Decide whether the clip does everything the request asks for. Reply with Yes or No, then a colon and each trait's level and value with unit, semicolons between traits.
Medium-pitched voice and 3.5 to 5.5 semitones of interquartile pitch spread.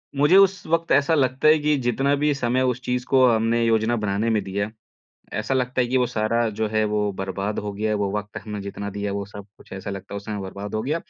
No: low, 110 Hz; average, 4.2 semitones